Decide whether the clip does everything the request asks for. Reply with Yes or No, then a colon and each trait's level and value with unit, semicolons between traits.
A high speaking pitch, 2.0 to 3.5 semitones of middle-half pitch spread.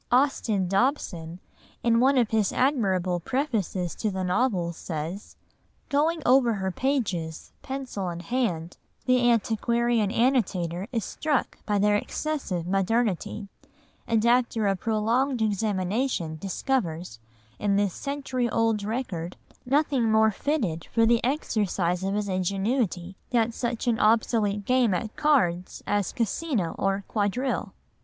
No: high, 215 Hz; average, 4.9 semitones